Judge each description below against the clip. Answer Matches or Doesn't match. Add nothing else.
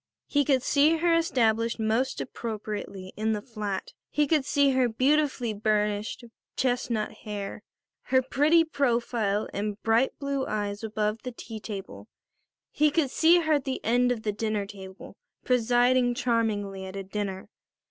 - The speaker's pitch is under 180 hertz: Doesn't match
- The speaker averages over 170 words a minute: Doesn't match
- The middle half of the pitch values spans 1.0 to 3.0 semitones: Doesn't match